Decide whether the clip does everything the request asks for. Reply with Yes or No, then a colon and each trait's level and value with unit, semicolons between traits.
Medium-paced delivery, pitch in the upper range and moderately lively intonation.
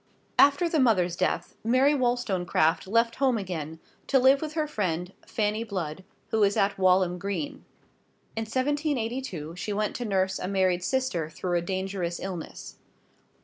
No: average, 150 wpm; high, 200 Hz; wide, 5.9 semitones